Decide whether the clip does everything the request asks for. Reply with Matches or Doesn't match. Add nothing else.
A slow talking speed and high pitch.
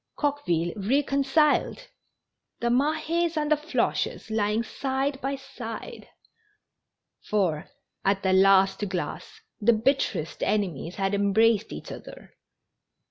Matches